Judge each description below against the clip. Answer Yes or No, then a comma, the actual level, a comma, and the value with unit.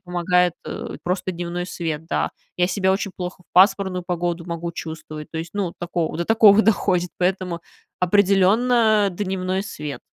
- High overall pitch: No, medium, 180 Hz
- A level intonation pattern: Yes, narrow, 2.2 semitones